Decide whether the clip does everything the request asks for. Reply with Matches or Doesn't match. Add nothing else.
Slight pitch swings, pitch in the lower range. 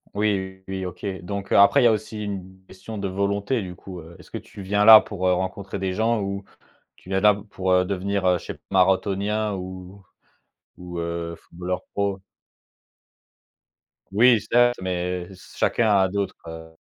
Matches